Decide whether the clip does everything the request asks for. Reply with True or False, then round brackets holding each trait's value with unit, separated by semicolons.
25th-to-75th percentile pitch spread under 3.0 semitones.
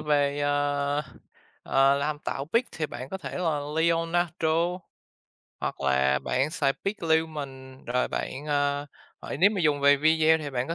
True (2.5 semitones)